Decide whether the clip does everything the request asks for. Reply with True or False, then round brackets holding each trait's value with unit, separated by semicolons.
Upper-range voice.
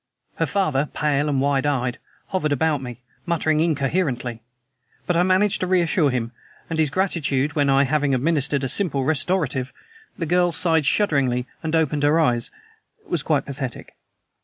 False (150 Hz)